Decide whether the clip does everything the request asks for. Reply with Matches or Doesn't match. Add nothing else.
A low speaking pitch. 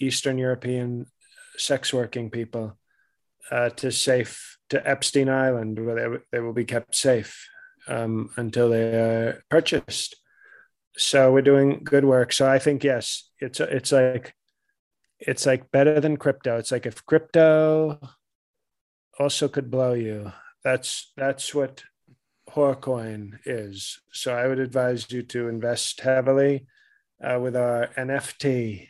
Matches